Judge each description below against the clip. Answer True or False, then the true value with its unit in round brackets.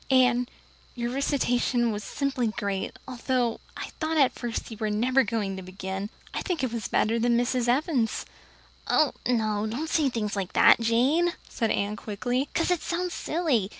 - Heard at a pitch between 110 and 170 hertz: False (240 Hz)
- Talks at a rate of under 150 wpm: False (175 wpm)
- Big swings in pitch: False (3.9 semitones)